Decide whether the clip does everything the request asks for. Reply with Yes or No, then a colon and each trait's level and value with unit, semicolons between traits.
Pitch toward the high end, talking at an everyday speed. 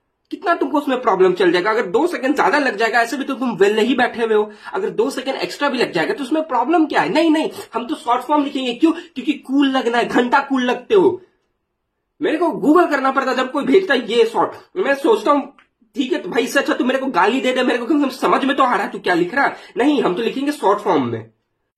No: very high, 280 Hz; fast, 260 wpm